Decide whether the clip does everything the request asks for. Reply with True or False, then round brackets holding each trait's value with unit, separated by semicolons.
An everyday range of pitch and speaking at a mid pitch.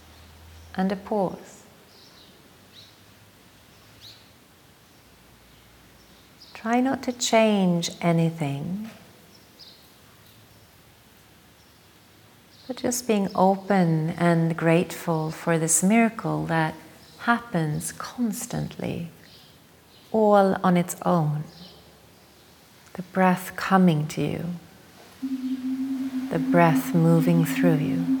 False (7.2 semitones; 170 Hz)